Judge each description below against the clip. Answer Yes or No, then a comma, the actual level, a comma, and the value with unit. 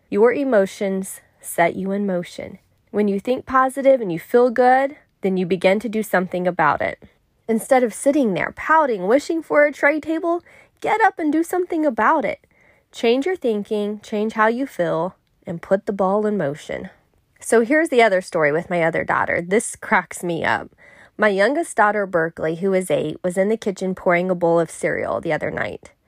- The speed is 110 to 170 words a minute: No, average, 195 wpm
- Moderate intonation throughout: No, wide, 6.6 semitones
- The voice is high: Yes, high, 215 Hz